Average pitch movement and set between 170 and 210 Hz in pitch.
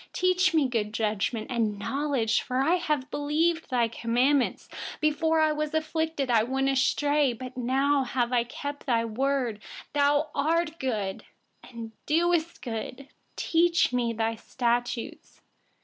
No: average, 4.5 semitones; very high, 270 Hz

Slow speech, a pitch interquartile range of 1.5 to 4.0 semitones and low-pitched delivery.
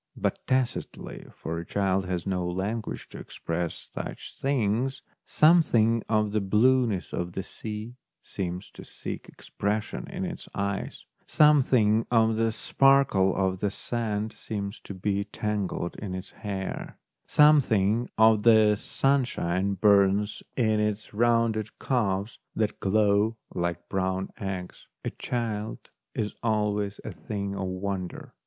Yes: slow, 130 wpm; average, 2.9 semitones; low, 105 Hz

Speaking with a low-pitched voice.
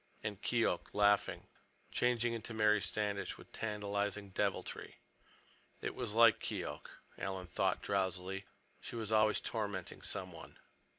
Yes: low, 105 Hz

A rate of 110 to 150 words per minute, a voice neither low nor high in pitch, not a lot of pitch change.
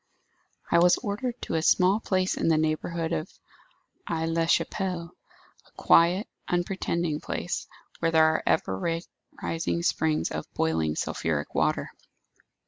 Yes: slow, 135 wpm; medium, 165 Hz; narrow, 2.1 semitones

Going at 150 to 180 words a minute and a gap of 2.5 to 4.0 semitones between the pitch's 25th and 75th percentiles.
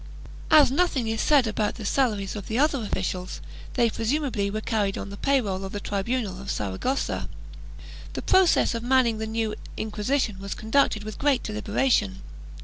No: average, 170 wpm; average, 4.4 semitones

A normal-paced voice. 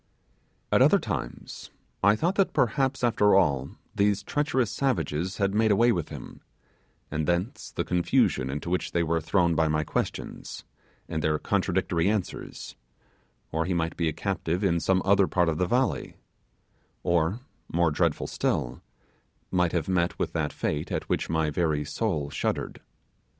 Yes: average, 160 wpm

